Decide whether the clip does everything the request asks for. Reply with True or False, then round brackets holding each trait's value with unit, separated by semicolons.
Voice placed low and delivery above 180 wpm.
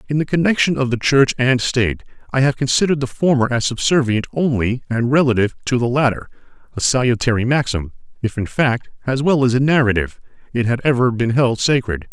True (125 Hz; 190 wpm)